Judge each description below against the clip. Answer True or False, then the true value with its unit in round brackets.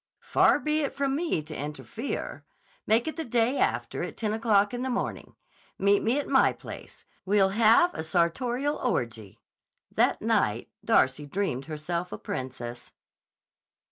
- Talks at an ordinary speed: True (150 wpm)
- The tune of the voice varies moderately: False (8.9 semitones)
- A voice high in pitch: True (205 Hz)